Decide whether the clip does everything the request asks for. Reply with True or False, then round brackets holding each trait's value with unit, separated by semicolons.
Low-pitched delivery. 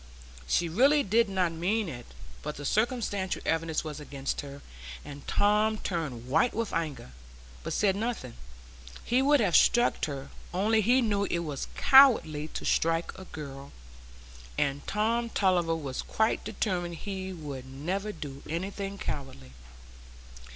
False (175 Hz)